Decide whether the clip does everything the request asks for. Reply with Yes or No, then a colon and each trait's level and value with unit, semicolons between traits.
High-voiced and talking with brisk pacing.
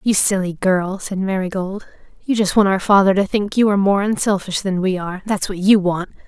Yes: high, 195 Hz; fast, 210 wpm